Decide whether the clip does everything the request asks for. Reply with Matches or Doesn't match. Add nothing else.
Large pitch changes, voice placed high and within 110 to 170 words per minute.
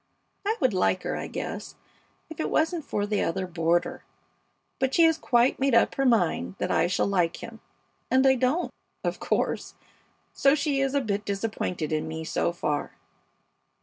Doesn't match